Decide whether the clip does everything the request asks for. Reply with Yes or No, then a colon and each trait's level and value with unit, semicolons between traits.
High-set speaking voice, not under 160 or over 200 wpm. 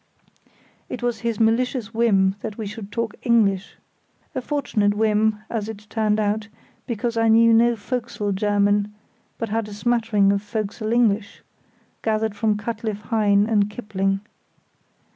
No: high, 215 Hz; average, 145 wpm